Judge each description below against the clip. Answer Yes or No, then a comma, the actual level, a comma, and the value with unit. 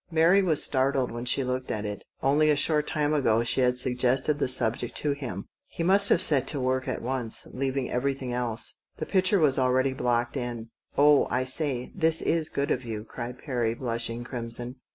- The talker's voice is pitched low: Yes, low, 130 Hz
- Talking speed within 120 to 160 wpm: No, average, 195 wpm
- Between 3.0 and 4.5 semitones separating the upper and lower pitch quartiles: Yes, average, 3.3 semitones